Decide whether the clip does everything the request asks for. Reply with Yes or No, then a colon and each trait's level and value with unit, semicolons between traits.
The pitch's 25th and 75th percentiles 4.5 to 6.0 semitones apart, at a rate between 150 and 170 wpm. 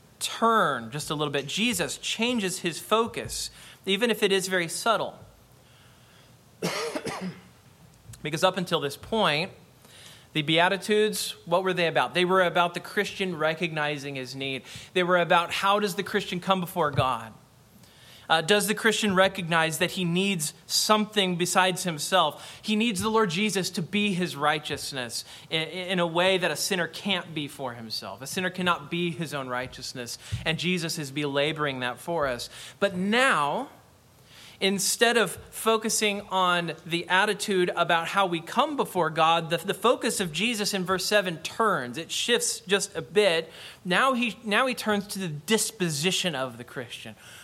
Yes: average, 4.8 semitones; average, 160 wpm